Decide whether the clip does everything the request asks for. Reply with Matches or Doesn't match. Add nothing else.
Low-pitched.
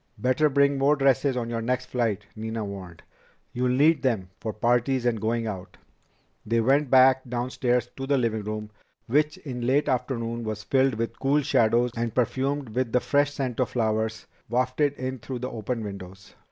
Matches